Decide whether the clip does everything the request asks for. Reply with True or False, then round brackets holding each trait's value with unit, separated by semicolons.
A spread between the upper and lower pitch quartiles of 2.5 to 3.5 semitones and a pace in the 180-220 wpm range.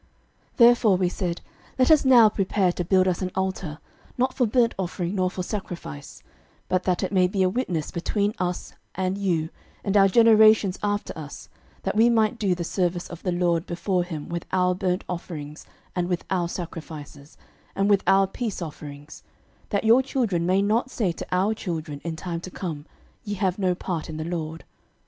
True (3.1 semitones; 195 wpm)